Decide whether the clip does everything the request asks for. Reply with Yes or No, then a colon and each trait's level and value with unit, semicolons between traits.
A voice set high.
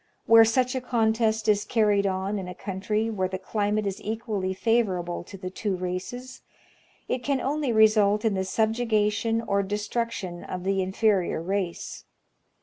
Yes: high, 210 Hz